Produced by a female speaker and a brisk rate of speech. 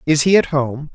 No: male; fast, 255 wpm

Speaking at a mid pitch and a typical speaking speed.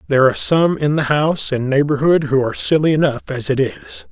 No: medium, 145 Hz; fast, 220 wpm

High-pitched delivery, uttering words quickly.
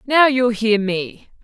No: high, 230 Hz; average, 165 wpm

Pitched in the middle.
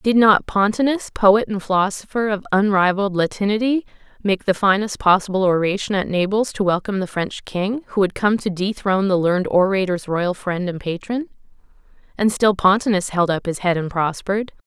No: high, 195 Hz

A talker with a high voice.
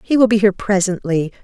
Yes: high, 200 Hz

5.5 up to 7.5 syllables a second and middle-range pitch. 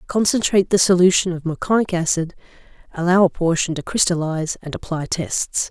Yes: 5.7 syllables/s; medium, 175 Hz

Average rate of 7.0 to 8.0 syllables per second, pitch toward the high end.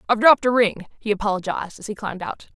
Yes: 7.7 syllables/s; high, 215 Hz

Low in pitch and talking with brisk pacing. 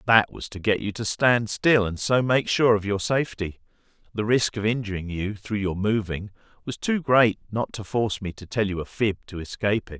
Yes: low, 105 Hz; fast, 230 wpm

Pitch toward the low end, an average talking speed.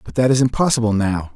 No: low, 115 Hz; fast, 220 wpm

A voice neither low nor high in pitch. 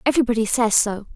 No: high, 230 Hz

